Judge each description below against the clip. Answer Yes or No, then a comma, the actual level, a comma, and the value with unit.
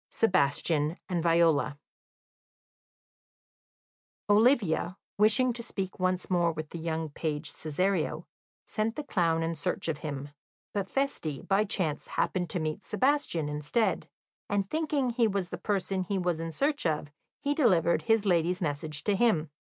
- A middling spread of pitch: Yes, average, 5.0 semitones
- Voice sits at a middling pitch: Yes, medium, 180 Hz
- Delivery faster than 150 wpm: No, average, 145 wpm